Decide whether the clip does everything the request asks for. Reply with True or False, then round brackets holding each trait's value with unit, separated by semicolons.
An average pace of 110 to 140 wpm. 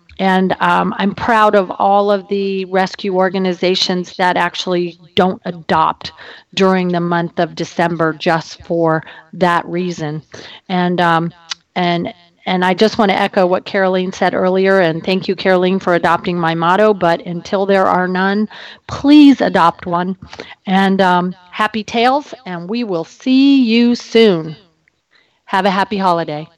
False (150 wpm)